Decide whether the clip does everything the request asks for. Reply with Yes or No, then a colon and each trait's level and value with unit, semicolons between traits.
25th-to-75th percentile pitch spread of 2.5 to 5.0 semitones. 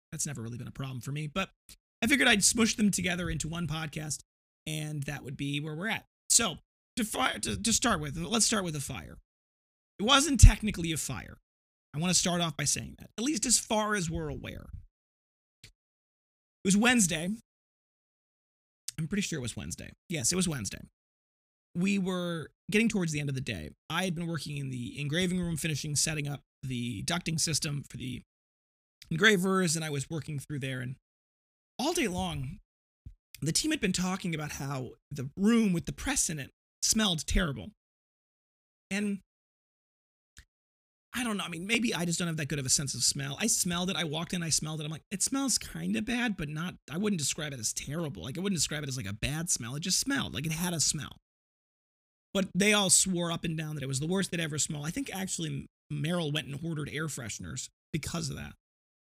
No: wide, 5.5 semitones